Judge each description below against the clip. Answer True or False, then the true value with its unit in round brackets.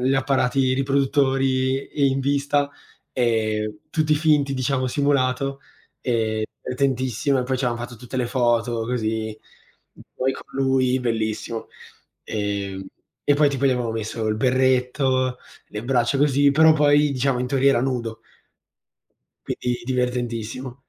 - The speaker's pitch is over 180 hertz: False (130 Hz)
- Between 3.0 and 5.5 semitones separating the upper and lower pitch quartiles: False (2.6 semitones)